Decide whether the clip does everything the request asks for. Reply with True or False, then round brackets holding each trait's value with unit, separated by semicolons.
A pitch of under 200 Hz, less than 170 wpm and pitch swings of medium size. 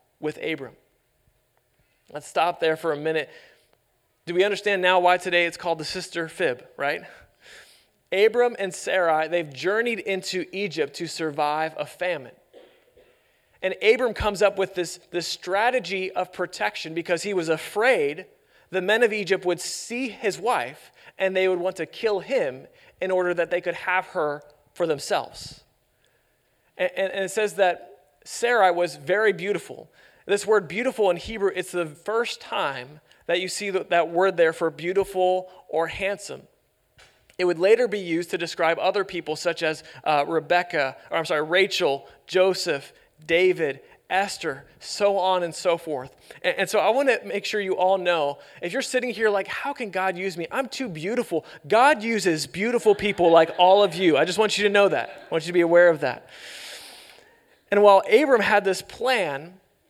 False (185 Hz; 175 wpm; 3.4 semitones)